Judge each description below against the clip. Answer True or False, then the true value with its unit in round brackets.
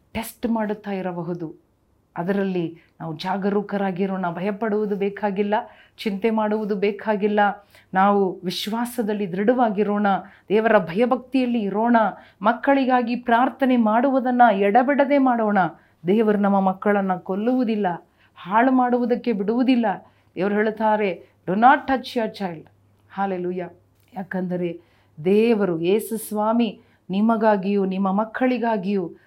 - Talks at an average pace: True (90 wpm)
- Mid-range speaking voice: False (210 Hz)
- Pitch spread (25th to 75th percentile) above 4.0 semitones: False (3.1 semitones)